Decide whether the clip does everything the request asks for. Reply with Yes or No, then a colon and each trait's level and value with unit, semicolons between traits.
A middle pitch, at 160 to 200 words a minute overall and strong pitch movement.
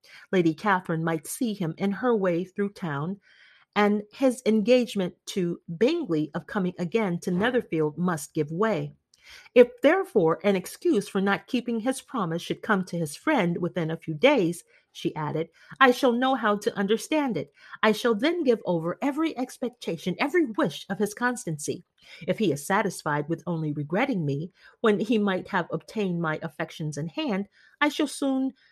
No: high, 195 Hz; average, 170 wpm; wide, 6.4 semitones